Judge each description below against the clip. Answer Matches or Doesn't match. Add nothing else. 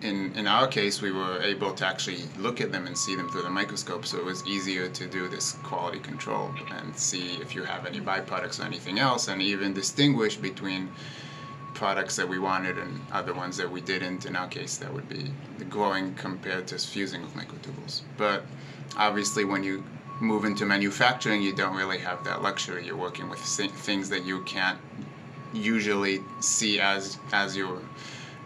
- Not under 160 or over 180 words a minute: Doesn't match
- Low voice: Matches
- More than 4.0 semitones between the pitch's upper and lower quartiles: Matches